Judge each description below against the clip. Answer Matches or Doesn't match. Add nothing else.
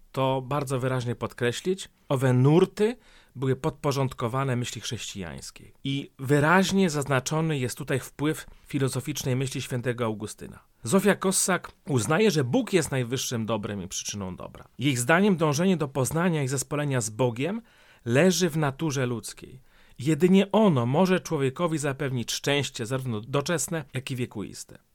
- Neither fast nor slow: Matches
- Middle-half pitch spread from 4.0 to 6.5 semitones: Matches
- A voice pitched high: Doesn't match